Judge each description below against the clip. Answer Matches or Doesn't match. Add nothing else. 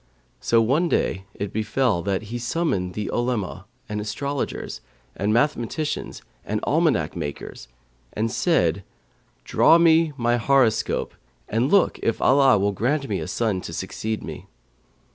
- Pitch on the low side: Matches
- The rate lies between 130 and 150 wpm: Matches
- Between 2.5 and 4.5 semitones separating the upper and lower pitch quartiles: Doesn't match